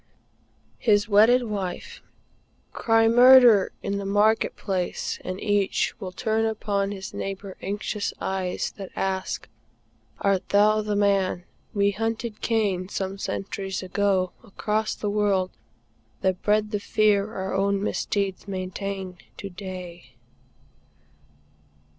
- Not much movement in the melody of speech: Yes, narrow, 1.9 semitones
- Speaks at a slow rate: Yes, slow, 115 wpm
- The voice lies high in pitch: Yes, high, 200 Hz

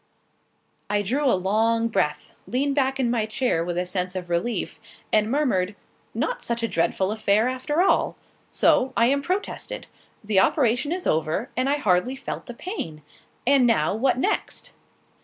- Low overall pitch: No, high, 230 Hz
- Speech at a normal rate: Yes, average, 165 wpm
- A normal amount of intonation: No, wide, 5.9 semitones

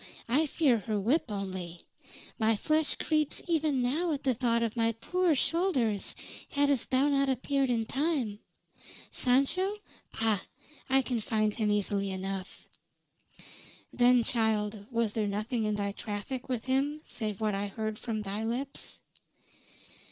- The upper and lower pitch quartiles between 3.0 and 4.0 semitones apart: No, average, 4.6 semitones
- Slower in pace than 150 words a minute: Yes, average, 140 wpm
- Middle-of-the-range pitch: No, high, 235 Hz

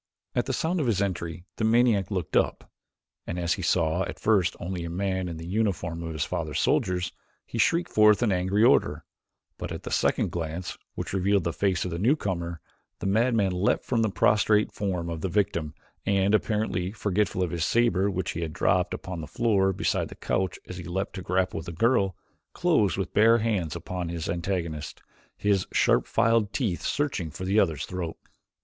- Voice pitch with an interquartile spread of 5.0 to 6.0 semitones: No, average, 3.7 semitones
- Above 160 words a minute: Yes, average, 195 wpm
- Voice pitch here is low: Yes, very low, 95 Hz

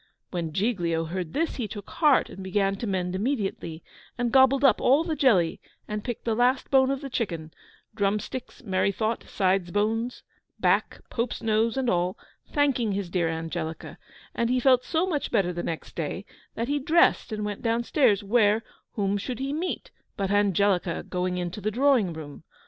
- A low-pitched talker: No, high, 210 Hz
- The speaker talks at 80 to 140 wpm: No, average, 185 wpm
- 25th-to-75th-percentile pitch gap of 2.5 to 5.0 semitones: No, wide, 5.4 semitones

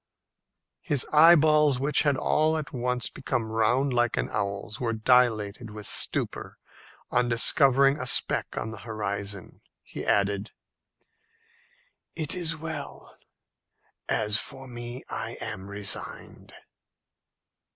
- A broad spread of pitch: No, average, 4.7 semitones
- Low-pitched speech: Yes, low, 120 Hz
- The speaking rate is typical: No, slow, 120 wpm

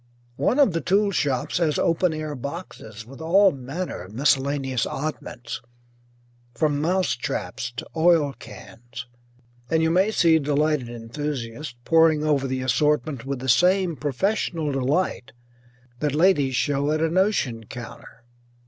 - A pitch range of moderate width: Yes, average, 4.2 semitones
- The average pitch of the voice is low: No, medium, 150 Hz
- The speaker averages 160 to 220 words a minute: No, average, 140 wpm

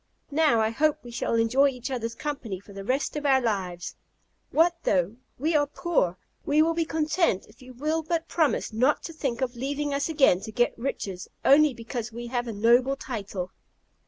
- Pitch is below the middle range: No, very high, 255 Hz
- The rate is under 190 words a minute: No, average, 195 wpm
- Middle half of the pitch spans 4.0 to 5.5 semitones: Yes, average, 4.8 semitones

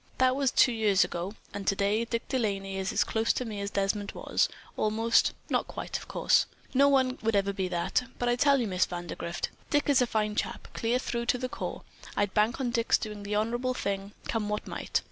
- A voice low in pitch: No, high, 220 Hz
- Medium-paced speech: No, fast, 220 wpm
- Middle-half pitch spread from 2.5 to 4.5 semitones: Yes, average, 3.6 semitones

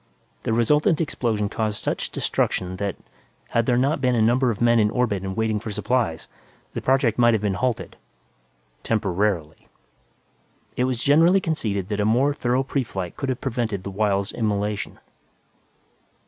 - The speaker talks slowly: No, average, 160 wpm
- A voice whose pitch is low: Yes, low, 110 Hz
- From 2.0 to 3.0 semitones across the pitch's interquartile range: No, average, 3.7 semitones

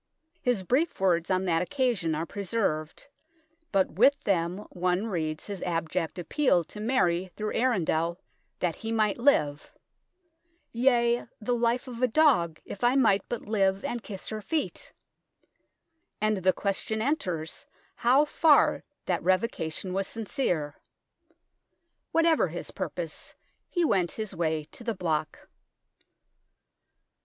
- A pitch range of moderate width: No, wide, 5.7 semitones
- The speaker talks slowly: Yes, slow, 130 wpm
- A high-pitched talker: Yes, high, 200 Hz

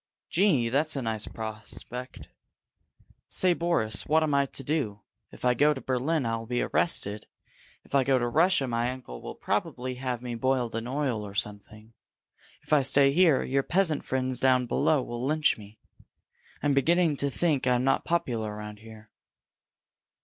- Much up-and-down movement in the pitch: No, average, 4.4 semitones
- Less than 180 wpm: Yes, average, 170 wpm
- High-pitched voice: No, low, 130 Hz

